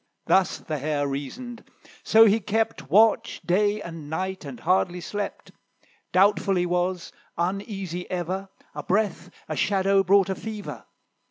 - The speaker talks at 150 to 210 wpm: No, average, 140 wpm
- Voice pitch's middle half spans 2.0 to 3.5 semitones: Yes, average, 3.0 semitones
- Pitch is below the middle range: No, high, 190 Hz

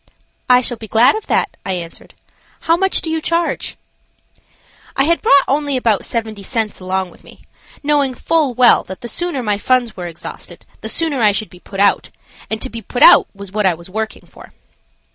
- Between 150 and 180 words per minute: No, average, 200 wpm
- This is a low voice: No, high, 230 Hz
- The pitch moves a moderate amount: No, wide, 5.8 semitones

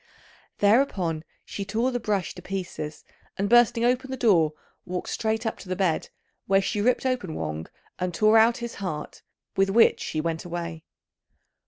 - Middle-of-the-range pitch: No, high, 195 Hz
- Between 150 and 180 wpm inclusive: Yes, average, 170 wpm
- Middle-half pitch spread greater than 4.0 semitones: Yes, average, 5.1 semitones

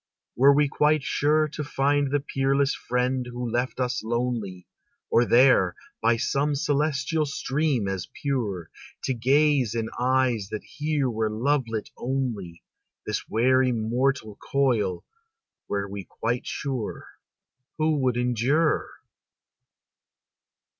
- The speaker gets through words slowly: Yes, slow, 120 wpm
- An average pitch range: Yes, average, 3.7 semitones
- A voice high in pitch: No, low, 130 Hz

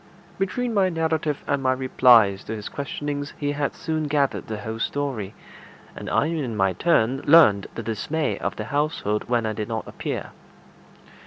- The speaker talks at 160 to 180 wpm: Yes, average, 170 wpm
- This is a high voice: No, low, 135 Hz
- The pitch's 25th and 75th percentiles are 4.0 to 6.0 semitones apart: Yes, wide, 5.5 semitones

